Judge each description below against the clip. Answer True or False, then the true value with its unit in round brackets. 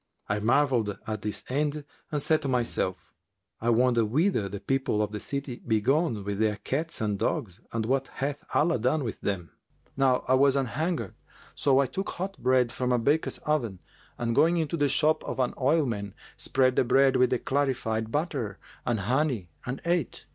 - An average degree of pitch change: True (4.7 semitones)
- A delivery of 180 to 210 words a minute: True (185 wpm)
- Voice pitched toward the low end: True (130 Hz)